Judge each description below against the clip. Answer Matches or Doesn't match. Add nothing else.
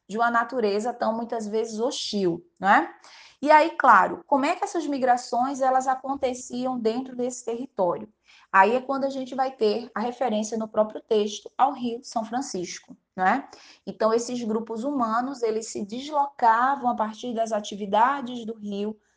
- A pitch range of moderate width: Matches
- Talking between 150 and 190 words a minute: Matches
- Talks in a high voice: Matches